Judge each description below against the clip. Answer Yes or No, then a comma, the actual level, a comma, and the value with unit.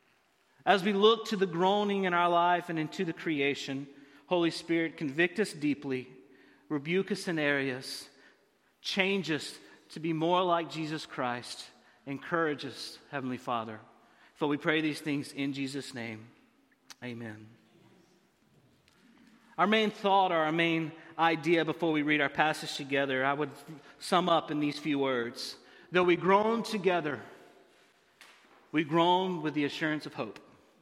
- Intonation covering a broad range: No, average, 3.9 semitones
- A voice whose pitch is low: No, medium, 155 Hz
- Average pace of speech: Yes, average, 145 wpm